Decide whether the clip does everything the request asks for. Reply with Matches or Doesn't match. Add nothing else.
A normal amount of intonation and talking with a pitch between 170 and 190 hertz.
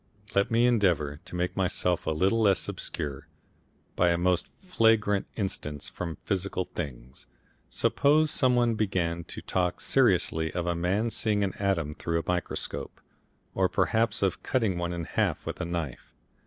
Doesn't match